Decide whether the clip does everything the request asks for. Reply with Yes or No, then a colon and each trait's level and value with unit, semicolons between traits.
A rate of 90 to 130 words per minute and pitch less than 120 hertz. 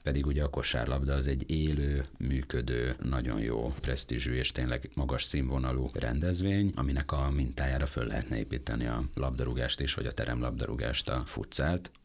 No: average, 150 wpm; very low, 65 Hz